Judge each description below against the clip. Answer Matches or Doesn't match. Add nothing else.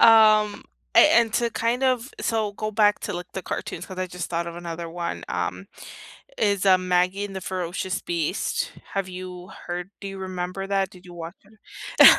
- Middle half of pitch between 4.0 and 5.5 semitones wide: Doesn't match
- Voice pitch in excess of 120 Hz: Matches